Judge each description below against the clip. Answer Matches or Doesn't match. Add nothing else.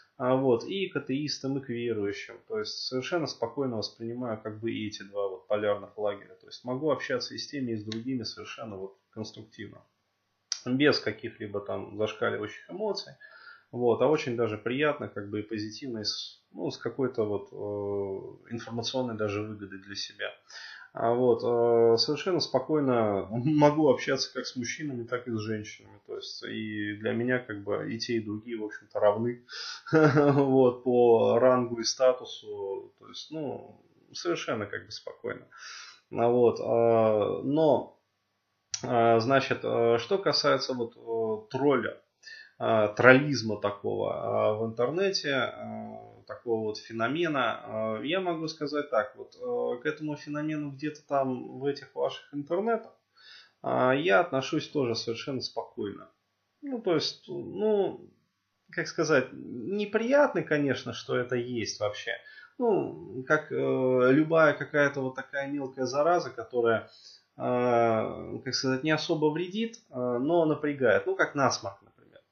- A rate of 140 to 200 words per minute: Doesn't match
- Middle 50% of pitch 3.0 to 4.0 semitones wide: Doesn't match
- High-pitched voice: Doesn't match